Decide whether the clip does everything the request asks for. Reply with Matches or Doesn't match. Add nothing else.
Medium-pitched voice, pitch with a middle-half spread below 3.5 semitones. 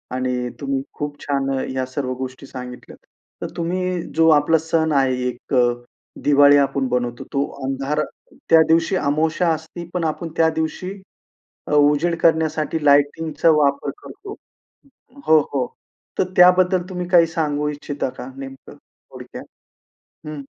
Matches